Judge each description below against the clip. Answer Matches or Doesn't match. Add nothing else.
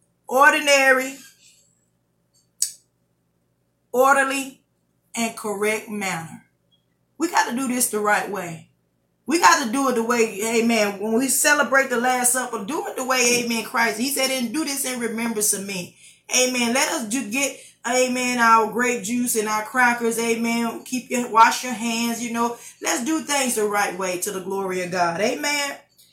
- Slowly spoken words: Doesn't match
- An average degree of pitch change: Matches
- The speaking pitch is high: Matches